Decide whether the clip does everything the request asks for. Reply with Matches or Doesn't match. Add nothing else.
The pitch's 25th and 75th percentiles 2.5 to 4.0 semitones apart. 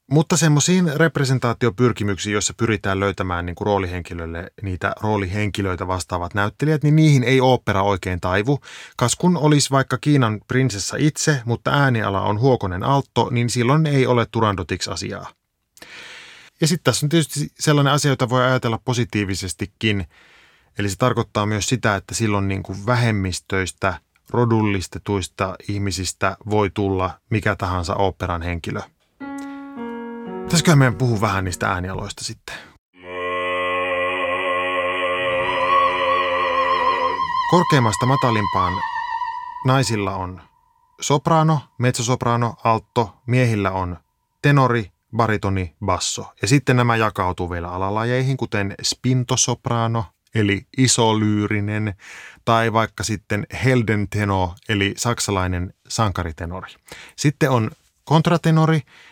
Doesn't match